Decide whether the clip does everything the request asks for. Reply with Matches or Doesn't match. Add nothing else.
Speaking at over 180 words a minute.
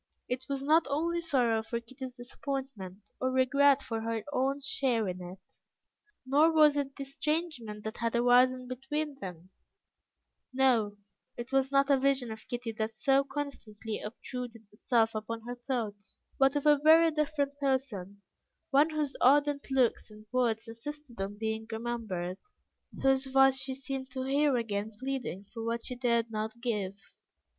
Doesn't match